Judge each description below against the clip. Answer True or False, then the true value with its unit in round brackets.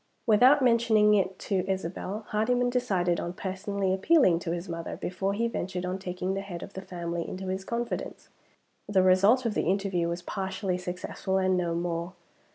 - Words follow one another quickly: False (175 wpm)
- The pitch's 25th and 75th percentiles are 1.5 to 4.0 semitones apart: True (2.8 semitones)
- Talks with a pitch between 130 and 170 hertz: False (190 Hz)